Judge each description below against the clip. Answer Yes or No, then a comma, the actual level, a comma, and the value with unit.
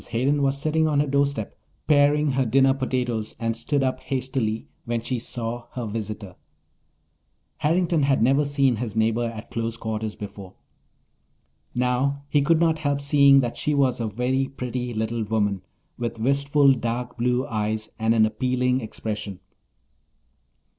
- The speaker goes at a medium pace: Yes, average, 150 wpm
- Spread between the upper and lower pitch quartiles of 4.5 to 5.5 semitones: No, average, 3.7 semitones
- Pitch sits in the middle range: No, low, 125 Hz